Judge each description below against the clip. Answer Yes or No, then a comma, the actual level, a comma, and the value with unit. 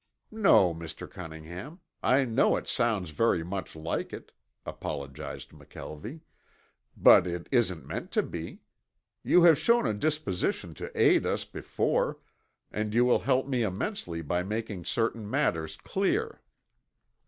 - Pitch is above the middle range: No, low, 105 Hz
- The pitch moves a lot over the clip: Yes, wide, 8.1 semitones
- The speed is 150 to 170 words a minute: No, slow, 135 wpm